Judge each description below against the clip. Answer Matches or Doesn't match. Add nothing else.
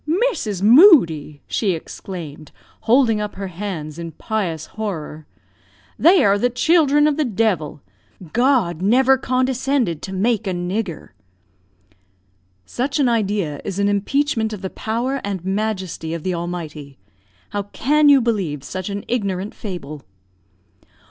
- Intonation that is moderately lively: Doesn't match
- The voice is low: Doesn't match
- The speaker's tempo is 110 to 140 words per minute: Matches